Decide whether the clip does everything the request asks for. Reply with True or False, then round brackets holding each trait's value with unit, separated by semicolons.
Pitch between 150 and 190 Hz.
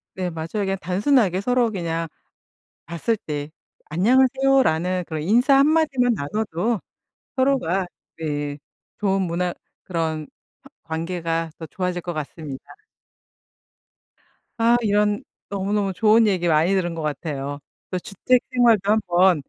True (185 Hz)